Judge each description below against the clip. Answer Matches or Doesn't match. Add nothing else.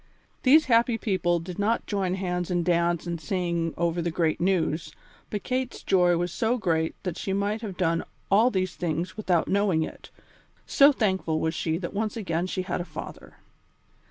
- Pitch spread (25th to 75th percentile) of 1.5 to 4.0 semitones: Matches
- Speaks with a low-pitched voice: Doesn't match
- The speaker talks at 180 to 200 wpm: Matches